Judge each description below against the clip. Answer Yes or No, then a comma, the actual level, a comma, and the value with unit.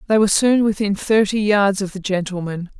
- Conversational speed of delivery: Yes, average, 195 wpm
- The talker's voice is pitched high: Yes, high, 200 Hz